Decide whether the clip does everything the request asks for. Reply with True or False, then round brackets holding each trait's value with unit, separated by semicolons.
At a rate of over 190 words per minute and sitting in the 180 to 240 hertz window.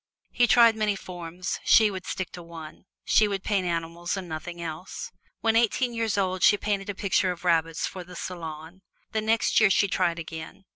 True (200 wpm; 185 Hz)